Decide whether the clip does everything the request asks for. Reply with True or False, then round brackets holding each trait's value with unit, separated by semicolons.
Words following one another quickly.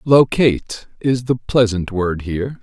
False (135 wpm)